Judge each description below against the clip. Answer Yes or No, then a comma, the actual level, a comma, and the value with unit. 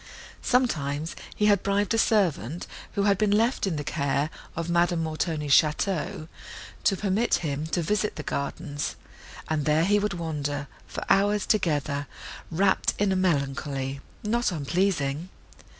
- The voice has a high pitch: No, medium, 170 Hz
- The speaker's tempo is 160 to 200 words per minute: No, average, 145 wpm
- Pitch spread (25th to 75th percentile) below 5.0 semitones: No, average, 5.3 semitones